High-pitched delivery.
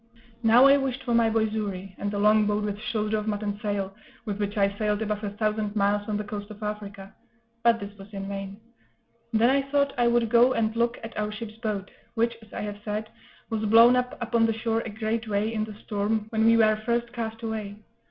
Yes: high, 215 Hz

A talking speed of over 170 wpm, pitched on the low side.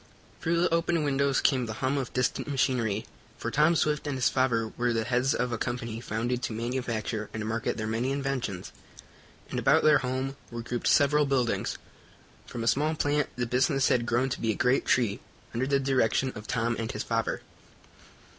Yes: average, 195 wpm; low, 125 Hz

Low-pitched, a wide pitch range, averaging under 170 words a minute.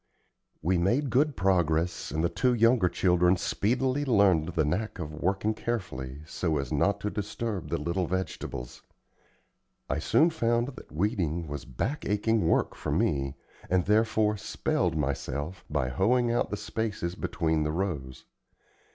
Yes: very low, 95 Hz; wide, 6.0 semitones; average, 150 wpm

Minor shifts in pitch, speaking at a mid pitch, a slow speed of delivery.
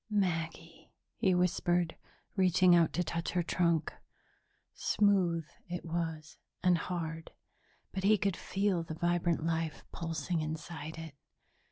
Yes: narrow, 1.8 semitones; medium, 170 Hz; slow, 125 wpm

